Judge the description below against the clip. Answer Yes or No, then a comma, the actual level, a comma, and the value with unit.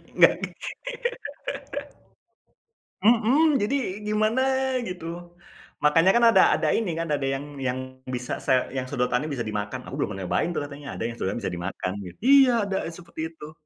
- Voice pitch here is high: No, medium, 150 Hz